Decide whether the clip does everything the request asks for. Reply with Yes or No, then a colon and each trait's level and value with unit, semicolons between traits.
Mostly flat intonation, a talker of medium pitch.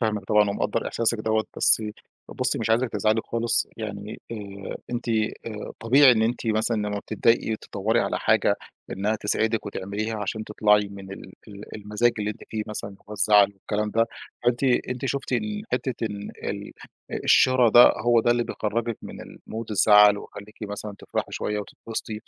No: narrow, 2.0 semitones; low, 110 Hz